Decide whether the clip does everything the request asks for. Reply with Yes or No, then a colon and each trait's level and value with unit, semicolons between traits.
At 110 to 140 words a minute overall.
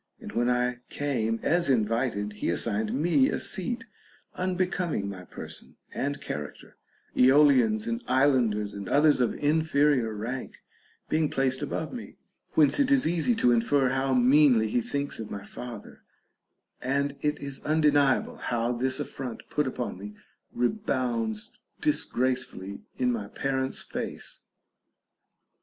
Yes: slow, 135 wpm